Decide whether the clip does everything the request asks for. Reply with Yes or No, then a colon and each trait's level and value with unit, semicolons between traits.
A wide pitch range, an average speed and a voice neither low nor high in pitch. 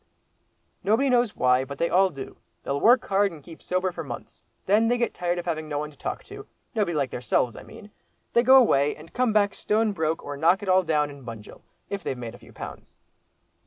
No: wide, 6.6 semitones; fast, 225 wpm; medium, 175 Hz